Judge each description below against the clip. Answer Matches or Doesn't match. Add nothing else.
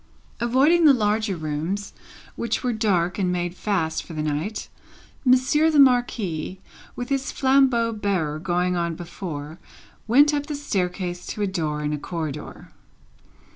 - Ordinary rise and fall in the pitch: Doesn't match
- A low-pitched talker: Doesn't match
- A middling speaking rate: Matches